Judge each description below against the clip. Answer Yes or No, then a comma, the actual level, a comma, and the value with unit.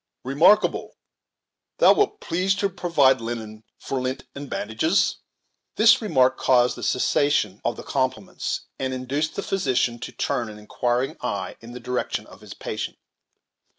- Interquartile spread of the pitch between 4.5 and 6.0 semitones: Yes, average, 4.9 semitones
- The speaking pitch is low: Yes, low, 130 Hz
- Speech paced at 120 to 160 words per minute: Yes, average, 150 wpm